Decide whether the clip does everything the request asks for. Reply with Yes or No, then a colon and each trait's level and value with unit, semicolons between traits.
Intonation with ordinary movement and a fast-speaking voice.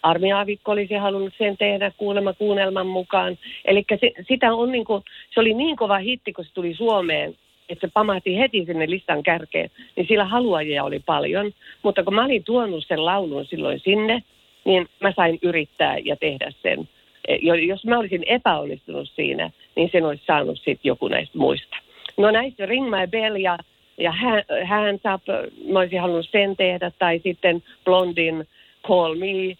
Yes: average, 3.0 semitones; fast, 170 wpm